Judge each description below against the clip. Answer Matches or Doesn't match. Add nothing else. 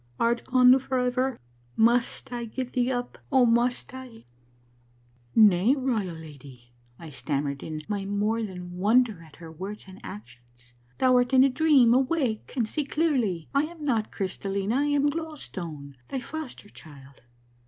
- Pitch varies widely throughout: Matches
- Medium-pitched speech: Doesn't match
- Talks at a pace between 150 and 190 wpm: Matches